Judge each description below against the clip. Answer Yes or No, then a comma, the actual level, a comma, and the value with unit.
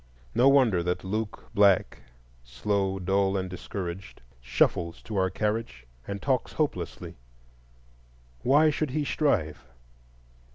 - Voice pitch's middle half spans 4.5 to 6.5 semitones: Yes, average, 5.1 semitones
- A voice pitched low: Yes, low, 100 Hz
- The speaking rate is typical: No, slow, 115 wpm